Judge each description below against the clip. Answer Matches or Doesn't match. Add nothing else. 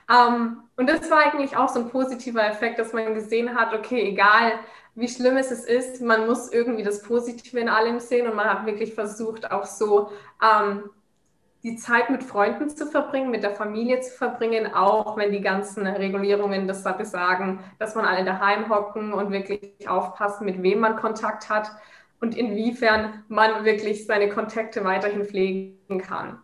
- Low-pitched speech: Doesn't match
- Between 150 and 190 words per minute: Matches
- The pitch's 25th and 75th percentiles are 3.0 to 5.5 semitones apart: Doesn't match